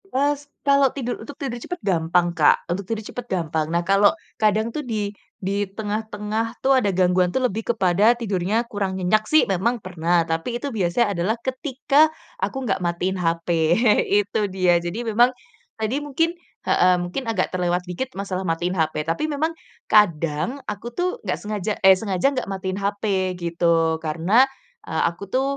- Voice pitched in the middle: No, high, 200 Hz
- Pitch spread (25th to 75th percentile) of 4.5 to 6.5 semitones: Yes, average, 5.1 semitones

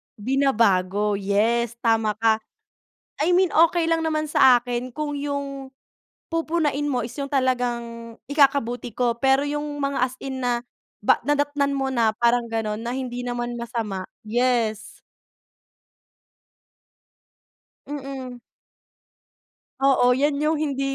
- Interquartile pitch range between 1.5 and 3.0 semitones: No, average, 3.4 semitones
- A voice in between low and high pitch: No, very high, 250 Hz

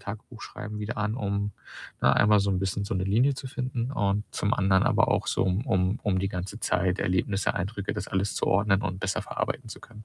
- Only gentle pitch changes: Yes, narrow, 2.0 semitones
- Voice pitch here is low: Yes, low, 100 Hz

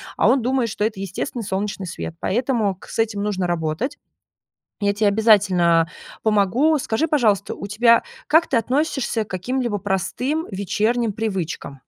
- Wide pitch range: No, average, 4.0 semitones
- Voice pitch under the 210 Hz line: No, high, 215 Hz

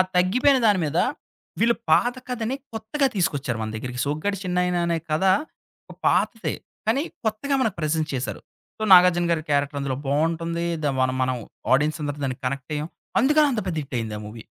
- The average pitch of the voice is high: No, medium, 165 Hz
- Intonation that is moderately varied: No, wide, 7.4 semitones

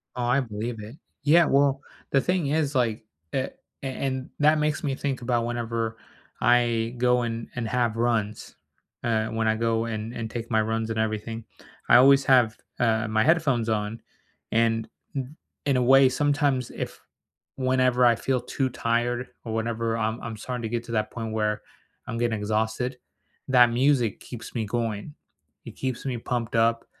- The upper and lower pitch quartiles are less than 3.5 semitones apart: Yes, narrow, 2.4 semitones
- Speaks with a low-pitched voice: Yes, low, 120 Hz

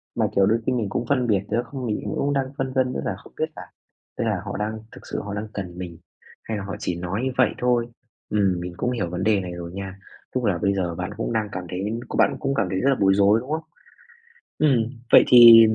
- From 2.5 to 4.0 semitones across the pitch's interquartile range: No, average, 4.5 semitones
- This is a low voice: Yes, low, 105 Hz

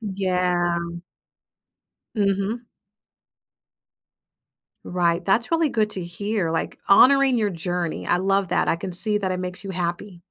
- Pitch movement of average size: Yes, average, 3.0 semitones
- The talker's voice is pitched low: No, high, 190 Hz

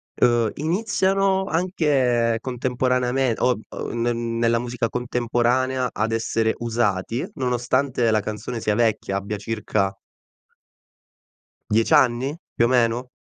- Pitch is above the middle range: No, low, 120 Hz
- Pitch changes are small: Yes, narrow, 2.1 semitones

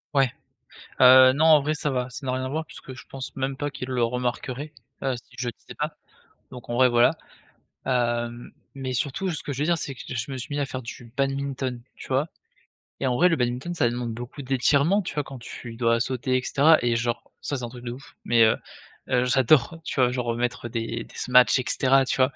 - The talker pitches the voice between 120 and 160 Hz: Yes, low, 130 Hz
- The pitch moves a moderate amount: No, narrow, 2.3 semitones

